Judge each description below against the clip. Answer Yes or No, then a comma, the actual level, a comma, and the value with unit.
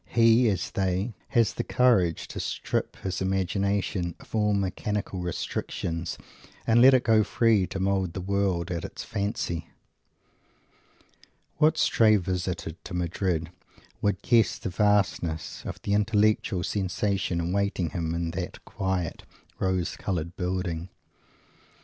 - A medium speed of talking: No, slow, 130 wpm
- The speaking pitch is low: Yes, very low, 95 Hz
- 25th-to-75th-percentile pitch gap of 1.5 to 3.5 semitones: Yes, average, 3.0 semitones